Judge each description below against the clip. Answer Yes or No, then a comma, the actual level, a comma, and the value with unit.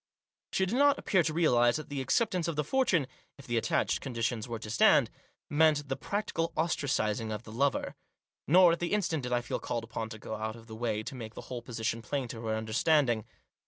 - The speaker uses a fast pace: Yes, fast, 230 wpm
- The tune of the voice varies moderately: No, wide, 6.0 semitones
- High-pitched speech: No, low, 125 Hz